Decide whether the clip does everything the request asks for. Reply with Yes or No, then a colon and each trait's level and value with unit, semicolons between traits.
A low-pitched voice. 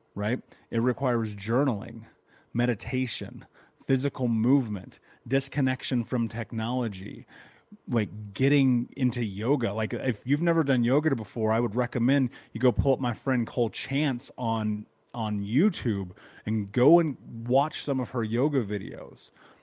Yes: low, 120 Hz